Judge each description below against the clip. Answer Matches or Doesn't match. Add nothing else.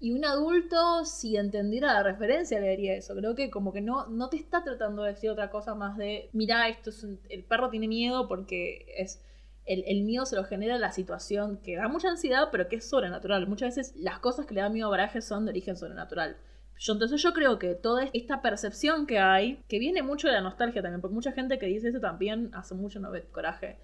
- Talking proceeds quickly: Matches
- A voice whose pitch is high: Matches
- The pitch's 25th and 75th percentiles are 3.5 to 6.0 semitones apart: Matches